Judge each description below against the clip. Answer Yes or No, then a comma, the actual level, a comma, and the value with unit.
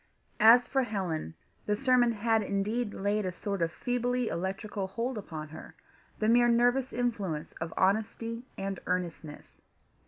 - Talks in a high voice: Yes, high, 210 Hz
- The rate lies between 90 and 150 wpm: Yes, average, 145 wpm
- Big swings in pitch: No, average, 4.2 semitones